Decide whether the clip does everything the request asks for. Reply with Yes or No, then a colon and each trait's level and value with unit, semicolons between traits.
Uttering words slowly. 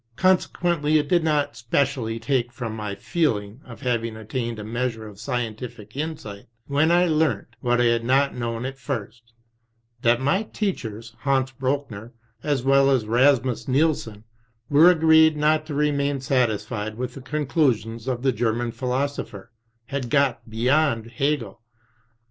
No: average, 155 wpm